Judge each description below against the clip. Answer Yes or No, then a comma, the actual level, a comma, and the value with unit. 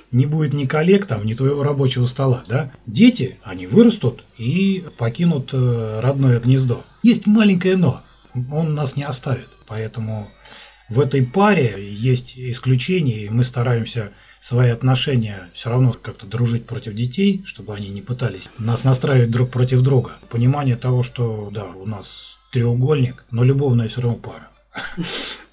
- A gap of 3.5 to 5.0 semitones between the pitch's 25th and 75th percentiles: No, average, 3.1 semitones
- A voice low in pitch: Yes, low, 125 Hz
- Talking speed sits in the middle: Yes, average, 145 wpm